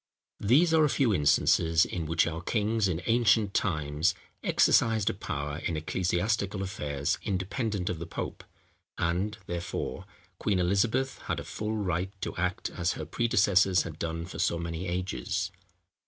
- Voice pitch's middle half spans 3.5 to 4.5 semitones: Yes, average, 4.2 semitones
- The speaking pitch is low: Yes, very low, 90 Hz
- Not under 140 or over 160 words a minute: Yes, average, 155 wpm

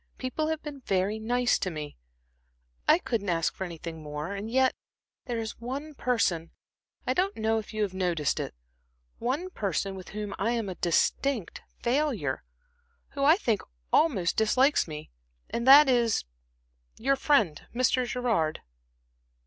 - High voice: Yes, high, 225 Hz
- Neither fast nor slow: Yes, average, 155 wpm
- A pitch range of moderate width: No, wide, 6.0 semitones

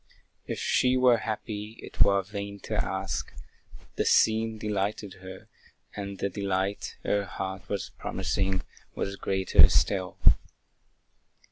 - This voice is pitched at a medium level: No, low, 100 Hz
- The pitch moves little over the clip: Yes, narrow, 1.9 semitones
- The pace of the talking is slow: Yes, slow, 120 wpm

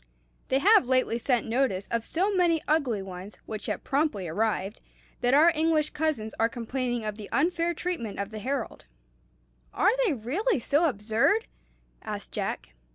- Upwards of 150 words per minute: Yes, average, 160 wpm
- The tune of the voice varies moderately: No, wide, 6.8 semitones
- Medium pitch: No, very high, 255 Hz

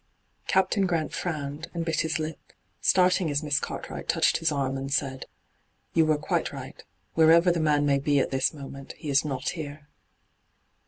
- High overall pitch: No, medium, 150 Hz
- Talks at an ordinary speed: Yes, average, 180 wpm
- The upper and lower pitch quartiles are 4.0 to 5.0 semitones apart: No, average, 2.7 semitones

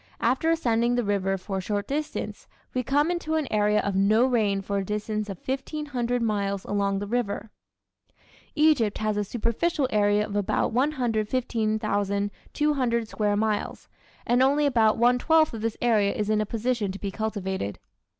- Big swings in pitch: No, average, 3.6 semitones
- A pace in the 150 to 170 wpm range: Yes, average, 165 wpm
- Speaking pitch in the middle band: No, high, 220 Hz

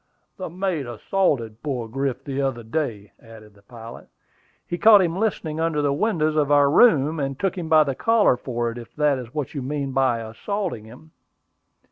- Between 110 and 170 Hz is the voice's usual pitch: Yes, medium, 140 Hz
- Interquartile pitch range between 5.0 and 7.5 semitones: Yes, wide, 5.4 semitones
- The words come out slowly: No, average, 190 wpm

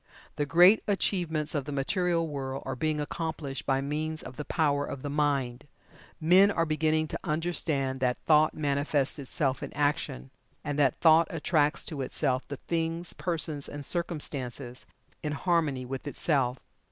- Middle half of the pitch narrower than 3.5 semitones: Yes, average, 2.9 semitones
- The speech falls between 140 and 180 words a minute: Yes, average, 155 wpm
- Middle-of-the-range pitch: Yes, medium, 150 Hz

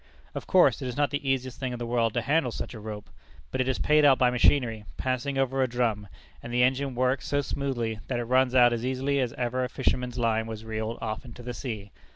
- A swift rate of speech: Yes, fast, 245 wpm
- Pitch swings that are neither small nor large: No, narrow, 2.2 semitones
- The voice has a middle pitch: No, low, 125 Hz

